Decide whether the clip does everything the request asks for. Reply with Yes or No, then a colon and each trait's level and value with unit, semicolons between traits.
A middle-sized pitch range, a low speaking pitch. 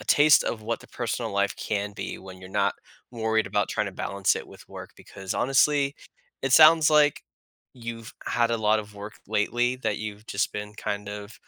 Yes: average, 3.2 semitones; low, 110 Hz